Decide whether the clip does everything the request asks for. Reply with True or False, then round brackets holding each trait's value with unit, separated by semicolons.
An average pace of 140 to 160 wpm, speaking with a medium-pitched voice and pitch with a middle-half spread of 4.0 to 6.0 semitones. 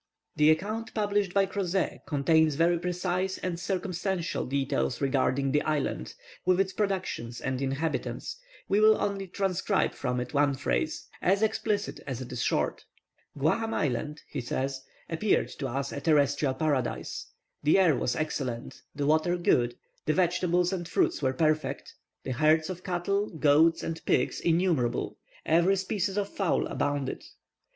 True (150 wpm; 165 Hz; 5.3 semitones)